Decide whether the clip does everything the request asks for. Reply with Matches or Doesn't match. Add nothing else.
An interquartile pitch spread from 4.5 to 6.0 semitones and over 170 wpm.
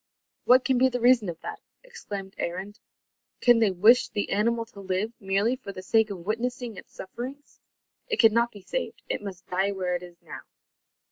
Doesn't match